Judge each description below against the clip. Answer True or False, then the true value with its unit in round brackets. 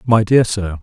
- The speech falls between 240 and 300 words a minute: False (220 wpm)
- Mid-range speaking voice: False (105 Hz)